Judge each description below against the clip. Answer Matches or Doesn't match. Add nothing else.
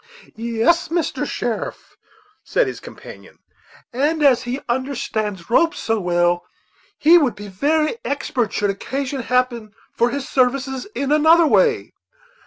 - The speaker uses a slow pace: Matches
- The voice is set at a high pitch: Matches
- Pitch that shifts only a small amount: Doesn't match